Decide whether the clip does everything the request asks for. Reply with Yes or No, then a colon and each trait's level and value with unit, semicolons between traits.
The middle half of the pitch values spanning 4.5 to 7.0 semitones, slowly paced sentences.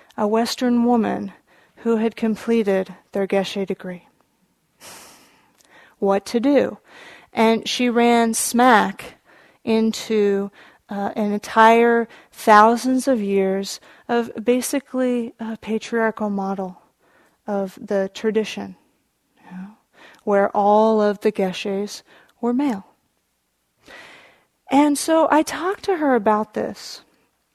No: average, 3.2 semitones; slow, 105 wpm